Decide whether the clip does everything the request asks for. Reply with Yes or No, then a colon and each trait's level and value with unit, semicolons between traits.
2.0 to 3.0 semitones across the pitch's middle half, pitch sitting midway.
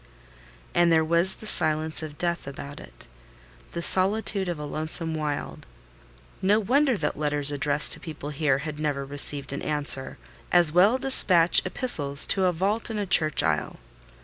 No: average, 4.1 semitones; medium, 160 Hz